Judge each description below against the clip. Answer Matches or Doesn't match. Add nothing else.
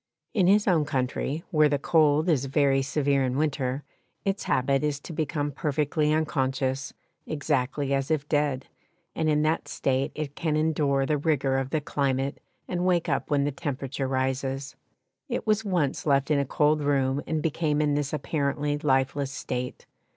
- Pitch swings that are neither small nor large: Doesn't match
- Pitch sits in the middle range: Matches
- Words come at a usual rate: Matches